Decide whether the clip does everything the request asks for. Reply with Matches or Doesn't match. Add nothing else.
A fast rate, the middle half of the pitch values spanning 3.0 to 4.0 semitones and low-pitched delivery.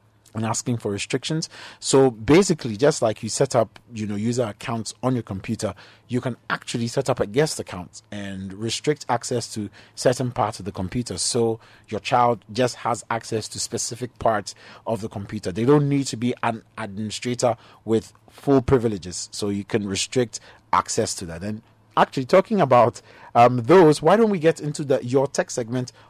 Doesn't match